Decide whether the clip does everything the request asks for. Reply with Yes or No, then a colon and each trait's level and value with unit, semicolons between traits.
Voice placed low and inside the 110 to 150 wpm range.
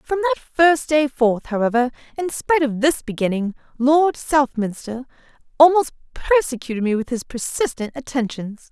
No: very high, 270 Hz; average, 140 wpm